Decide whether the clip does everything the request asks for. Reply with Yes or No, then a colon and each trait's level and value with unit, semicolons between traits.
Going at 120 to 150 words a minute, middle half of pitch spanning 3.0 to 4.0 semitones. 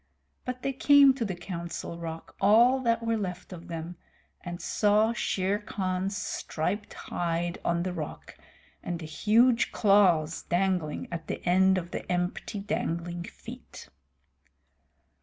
Yes: average, 140 wpm; average, 3.7 semitones